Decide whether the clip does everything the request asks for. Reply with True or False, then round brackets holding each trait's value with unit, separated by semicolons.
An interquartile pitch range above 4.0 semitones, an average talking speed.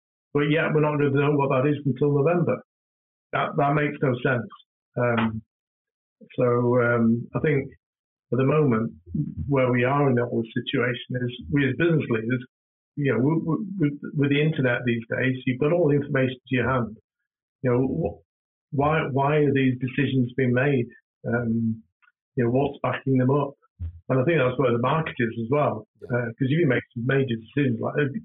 False (3.1 semitones; 195 wpm)